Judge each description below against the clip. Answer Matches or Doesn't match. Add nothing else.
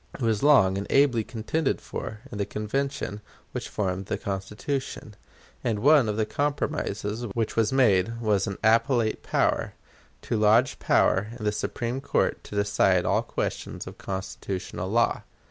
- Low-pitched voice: Matches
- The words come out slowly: Doesn't match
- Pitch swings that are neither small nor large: Matches